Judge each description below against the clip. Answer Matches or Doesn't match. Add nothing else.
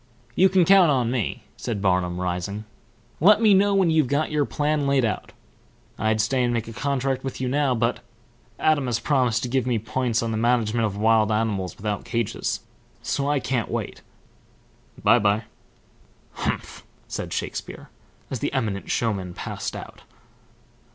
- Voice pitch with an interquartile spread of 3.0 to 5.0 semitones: Matches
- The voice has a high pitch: Doesn't match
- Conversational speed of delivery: Matches